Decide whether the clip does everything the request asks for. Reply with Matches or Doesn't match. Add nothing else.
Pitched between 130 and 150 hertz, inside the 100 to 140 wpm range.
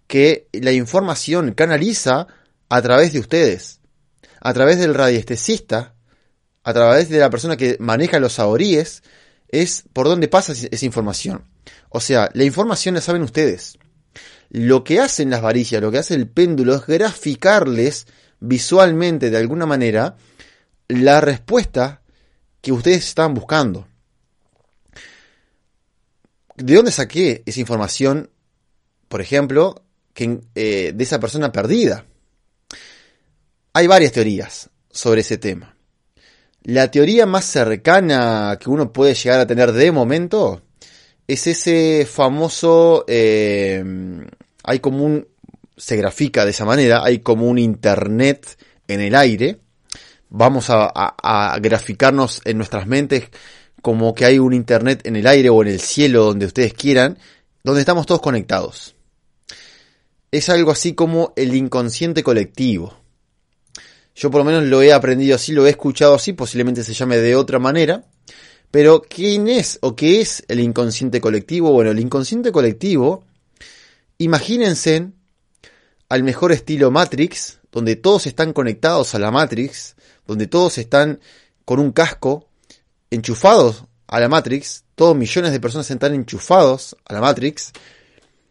Matches